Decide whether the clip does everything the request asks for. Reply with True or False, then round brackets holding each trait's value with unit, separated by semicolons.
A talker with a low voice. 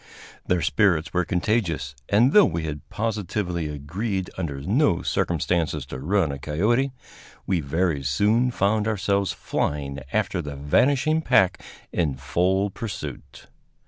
True (90 Hz)